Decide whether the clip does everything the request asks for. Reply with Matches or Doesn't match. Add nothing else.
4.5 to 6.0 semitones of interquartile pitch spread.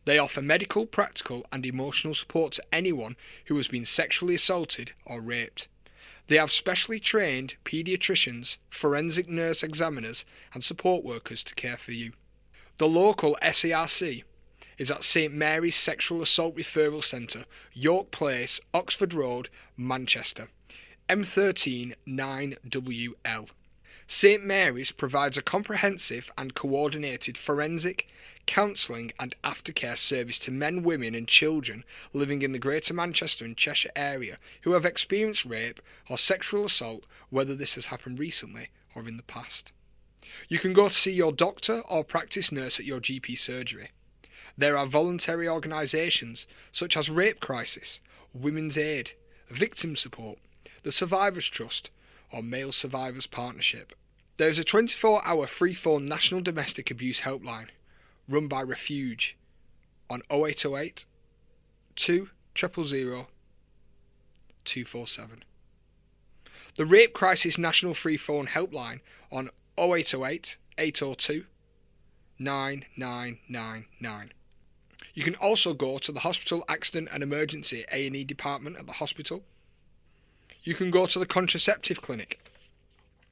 Matches